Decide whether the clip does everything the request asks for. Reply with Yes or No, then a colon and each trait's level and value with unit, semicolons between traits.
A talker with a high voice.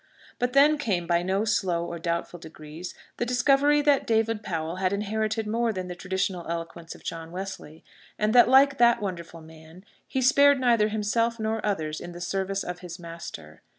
Yes: high, 195 Hz